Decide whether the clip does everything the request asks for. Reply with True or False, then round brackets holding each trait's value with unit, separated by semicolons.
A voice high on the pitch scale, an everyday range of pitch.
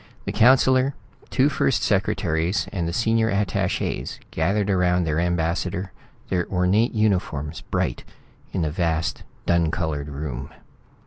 False (90 Hz; 4.1 semitones)